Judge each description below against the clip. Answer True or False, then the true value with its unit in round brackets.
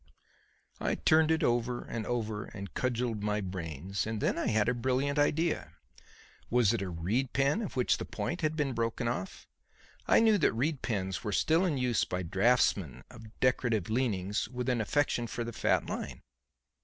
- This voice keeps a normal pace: True (180 wpm)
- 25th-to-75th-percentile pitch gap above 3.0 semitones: True (4.2 semitones)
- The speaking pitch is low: True (120 Hz)